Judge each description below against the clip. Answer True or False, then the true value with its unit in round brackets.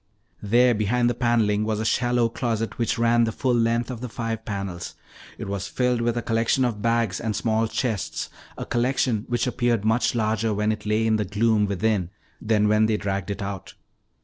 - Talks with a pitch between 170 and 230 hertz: False (115 Hz)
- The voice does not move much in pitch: True (2.1 semitones)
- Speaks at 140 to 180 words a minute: False (200 wpm)